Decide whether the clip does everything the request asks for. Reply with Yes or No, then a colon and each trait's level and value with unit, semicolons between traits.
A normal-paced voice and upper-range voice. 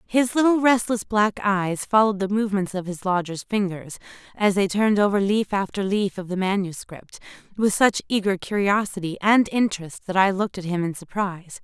Yes: average, 180 wpm; high, 200 Hz